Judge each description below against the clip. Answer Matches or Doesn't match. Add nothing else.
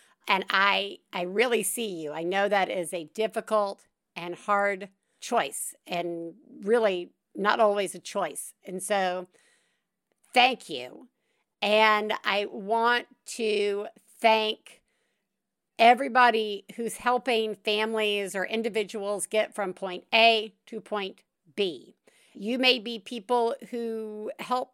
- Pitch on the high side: Matches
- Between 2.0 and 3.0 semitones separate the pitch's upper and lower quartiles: Matches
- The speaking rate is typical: Doesn't match